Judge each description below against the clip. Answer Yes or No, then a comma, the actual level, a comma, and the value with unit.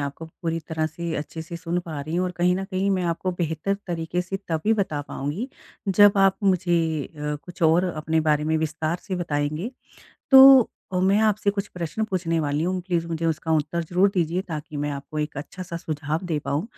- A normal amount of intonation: Yes, average, 3.0 semitones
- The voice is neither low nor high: Yes, medium, 170 Hz